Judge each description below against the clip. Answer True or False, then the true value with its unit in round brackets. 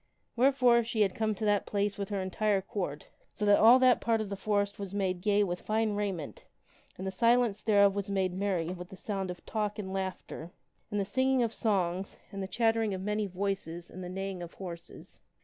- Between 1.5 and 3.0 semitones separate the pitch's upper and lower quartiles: True (2.4 semitones)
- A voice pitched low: False (200 Hz)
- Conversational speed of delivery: False (215 wpm)